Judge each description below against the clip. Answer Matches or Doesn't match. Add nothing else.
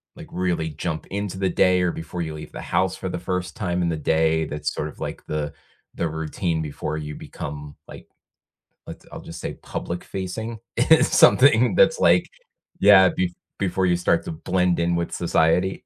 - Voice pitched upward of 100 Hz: Doesn't match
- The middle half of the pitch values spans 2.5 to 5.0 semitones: Matches